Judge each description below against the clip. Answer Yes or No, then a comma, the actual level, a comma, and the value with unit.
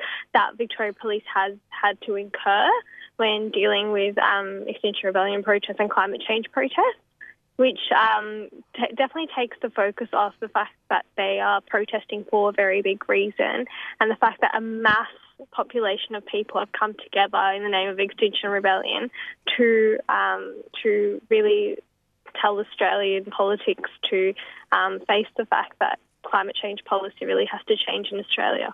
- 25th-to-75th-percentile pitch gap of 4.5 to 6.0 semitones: No, average, 3.8 semitones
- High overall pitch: Yes, high, 215 Hz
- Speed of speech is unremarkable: Yes, average, 160 wpm